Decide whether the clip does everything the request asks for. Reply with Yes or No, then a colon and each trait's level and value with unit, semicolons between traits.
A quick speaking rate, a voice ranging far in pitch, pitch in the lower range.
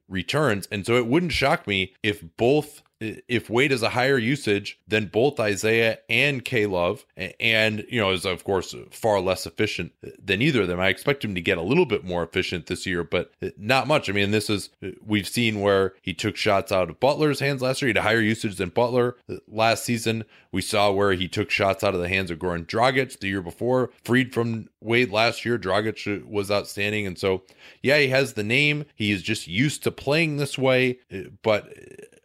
No: fast, 210 wpm; average, 4.3 semitones; low, 110 Hz